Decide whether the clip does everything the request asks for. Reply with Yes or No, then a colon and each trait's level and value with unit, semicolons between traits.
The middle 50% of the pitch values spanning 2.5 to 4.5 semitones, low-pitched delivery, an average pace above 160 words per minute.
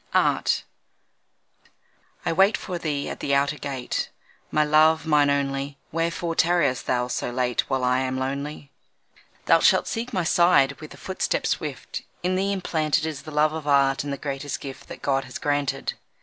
No: average, 2.9 semitones; medium, 145 Hz; average, 175 wpm